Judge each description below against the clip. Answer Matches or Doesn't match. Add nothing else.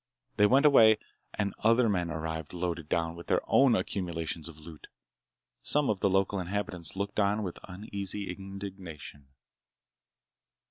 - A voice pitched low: Matches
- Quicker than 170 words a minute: Doesn't match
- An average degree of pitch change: Matches